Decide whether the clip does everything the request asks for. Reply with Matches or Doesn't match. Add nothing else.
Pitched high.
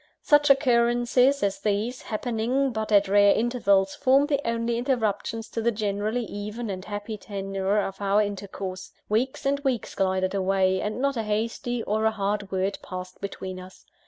Matches